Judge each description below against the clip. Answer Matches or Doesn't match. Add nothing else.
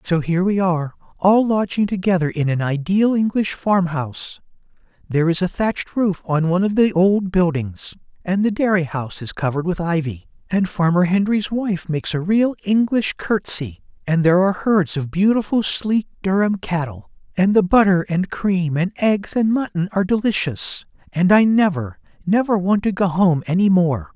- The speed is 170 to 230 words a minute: Matches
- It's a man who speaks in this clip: Matches